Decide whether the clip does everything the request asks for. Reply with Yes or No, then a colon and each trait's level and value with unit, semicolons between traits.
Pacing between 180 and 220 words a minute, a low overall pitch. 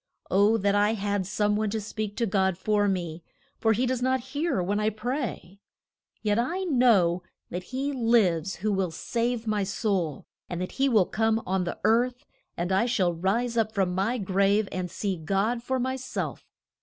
No: average, 190 wpm; high, 210 Hz